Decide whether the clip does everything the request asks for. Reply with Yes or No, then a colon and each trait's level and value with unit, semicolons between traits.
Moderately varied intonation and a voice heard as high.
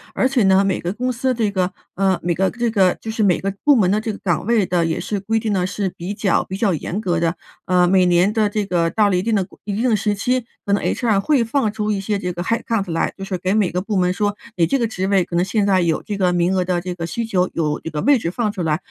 Yes: average, 3.2 semitones; high, 195 Hz